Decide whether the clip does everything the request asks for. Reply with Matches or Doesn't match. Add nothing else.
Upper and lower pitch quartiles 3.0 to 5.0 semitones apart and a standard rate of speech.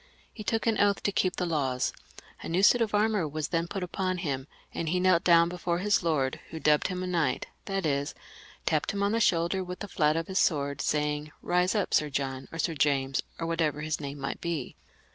Doesn't match